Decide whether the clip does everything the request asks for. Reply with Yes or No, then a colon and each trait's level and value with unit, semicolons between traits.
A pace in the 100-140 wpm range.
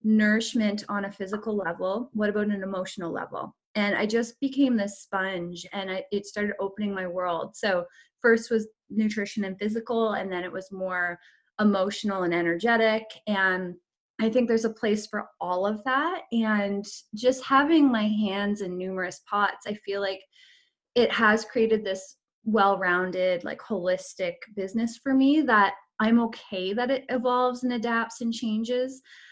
No: average, 160 wpm